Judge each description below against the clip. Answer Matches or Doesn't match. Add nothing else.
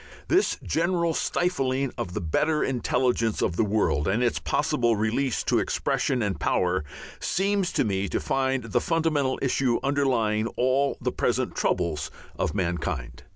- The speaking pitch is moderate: Doesn't match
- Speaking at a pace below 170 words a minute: Matches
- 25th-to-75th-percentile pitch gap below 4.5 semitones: Doesn't match